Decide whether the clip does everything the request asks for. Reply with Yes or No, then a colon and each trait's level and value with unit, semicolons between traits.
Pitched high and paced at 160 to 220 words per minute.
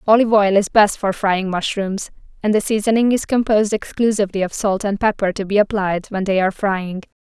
Yes: high, 205 Hz; average, 200 wpm